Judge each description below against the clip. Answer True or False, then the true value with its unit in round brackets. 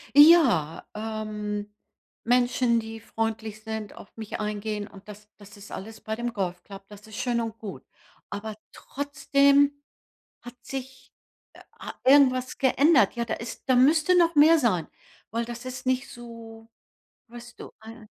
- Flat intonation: False (3.4 semitones)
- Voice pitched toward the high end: True (230 Hz)